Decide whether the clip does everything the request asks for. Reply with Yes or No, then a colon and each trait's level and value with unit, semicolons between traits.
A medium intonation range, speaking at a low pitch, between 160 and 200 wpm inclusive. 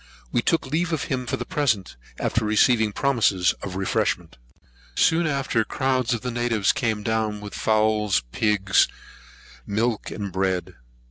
No: average, 3.6 semitones; low, 110 Hz; average, 150 wpm